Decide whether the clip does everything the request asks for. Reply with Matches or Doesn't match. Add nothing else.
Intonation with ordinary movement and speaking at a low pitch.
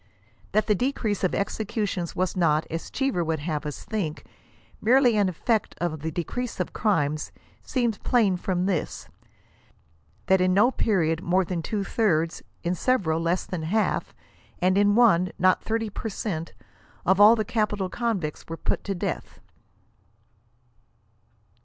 Doesn't match